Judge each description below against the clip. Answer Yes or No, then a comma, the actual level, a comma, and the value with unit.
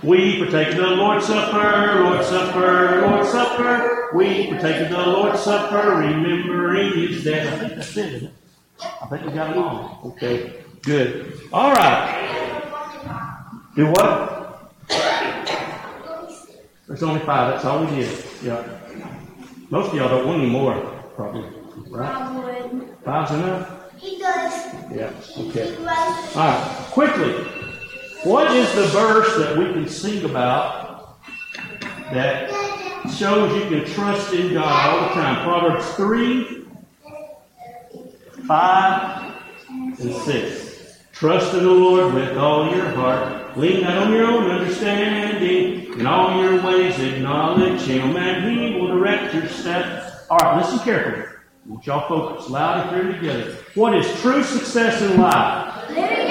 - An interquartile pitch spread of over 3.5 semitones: Yes, average, 5.3 semitones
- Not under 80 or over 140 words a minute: Yes, slow, 135 wpm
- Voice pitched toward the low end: No, medium, 185 Hz